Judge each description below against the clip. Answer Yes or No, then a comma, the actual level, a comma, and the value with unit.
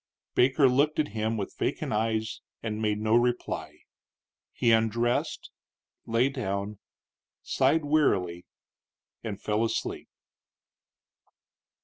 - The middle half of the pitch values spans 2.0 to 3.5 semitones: Yes, average, 3.0 semitones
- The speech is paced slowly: Yes, slow, 100 wpm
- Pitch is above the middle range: No, low, 115 Hz